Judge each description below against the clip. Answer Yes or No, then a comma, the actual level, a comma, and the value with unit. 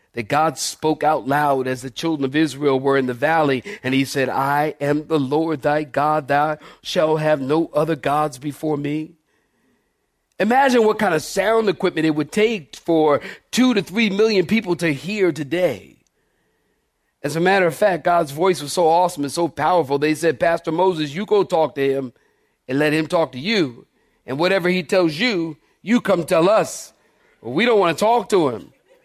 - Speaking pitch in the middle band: Yes, medium, 155 Hz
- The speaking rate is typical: Yes, average, 190 wpm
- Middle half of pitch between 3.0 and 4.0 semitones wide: Yes, average, 3.7 semitones